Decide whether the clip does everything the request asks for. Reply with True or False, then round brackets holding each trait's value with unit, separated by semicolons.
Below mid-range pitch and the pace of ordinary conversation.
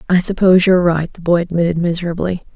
False (175 Hz; 190 wpm)